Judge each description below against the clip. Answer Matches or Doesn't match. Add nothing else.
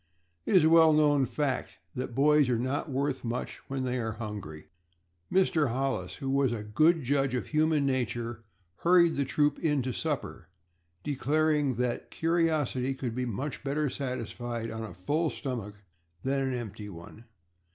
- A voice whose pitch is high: Doesn't match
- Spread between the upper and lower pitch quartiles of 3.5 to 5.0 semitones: Matches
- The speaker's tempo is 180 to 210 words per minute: Doesn't match